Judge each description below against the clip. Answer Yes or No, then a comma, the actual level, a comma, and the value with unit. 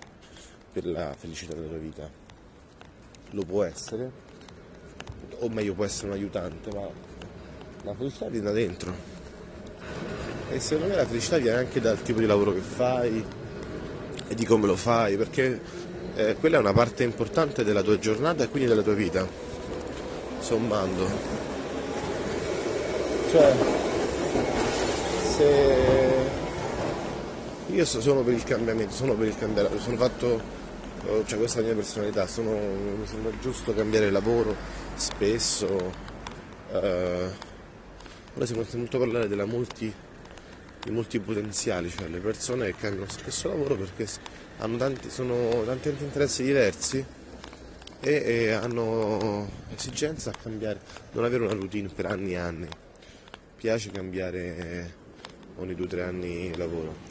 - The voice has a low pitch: Yes, low, 110 Hz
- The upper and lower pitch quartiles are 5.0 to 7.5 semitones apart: No, average, 4.3 semitones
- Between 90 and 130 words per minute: No, average, 140 wpm